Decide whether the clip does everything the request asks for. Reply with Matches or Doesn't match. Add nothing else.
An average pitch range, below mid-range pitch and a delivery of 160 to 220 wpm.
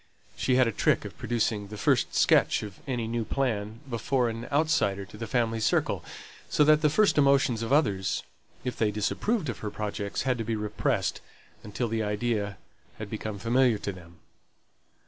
Matches